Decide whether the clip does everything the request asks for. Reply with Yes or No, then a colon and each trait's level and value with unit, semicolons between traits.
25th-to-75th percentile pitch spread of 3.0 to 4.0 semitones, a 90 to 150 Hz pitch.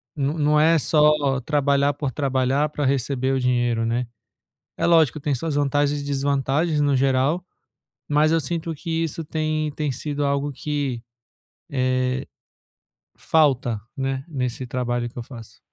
No: narrow, 2.5 semitones; medium, 140 Hz